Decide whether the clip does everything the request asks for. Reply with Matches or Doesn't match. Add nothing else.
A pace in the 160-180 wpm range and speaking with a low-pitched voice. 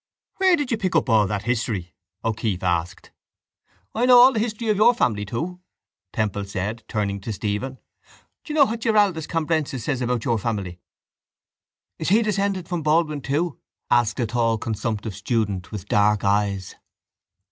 Matches